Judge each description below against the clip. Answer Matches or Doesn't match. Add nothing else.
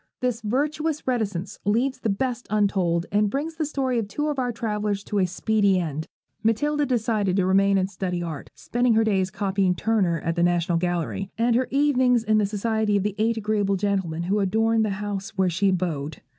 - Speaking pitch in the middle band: Doesn't match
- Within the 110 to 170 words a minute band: Doesn't match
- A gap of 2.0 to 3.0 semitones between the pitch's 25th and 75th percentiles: Doesn't match